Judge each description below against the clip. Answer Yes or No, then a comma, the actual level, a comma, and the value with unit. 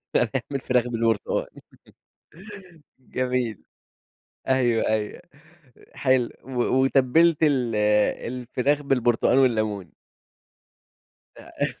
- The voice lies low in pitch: Yes, low, 125 Hz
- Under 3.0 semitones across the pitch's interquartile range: Yes, narrow, 2.4 semitones